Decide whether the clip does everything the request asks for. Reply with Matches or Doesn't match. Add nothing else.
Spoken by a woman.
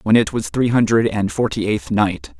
Doesn't match